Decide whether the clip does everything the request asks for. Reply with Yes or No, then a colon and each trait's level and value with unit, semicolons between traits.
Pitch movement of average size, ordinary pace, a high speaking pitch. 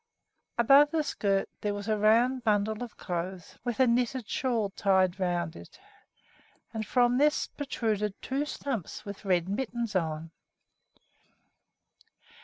No: average, 4.4 semitones; slow, 130 wpm; high, 215 Hz